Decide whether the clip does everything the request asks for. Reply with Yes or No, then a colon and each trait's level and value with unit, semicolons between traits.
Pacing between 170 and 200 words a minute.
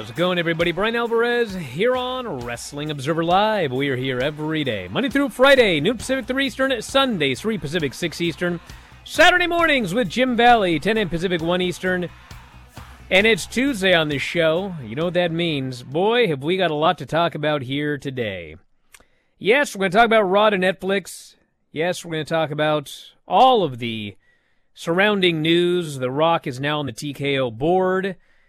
Yes: average, 185 wpm